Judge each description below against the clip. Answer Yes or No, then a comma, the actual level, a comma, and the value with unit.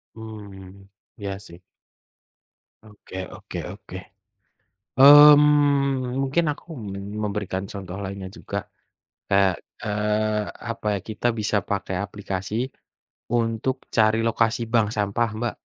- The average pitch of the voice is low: Yes, low, 110 Hz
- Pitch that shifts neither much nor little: Yes, average, 3.2 semitones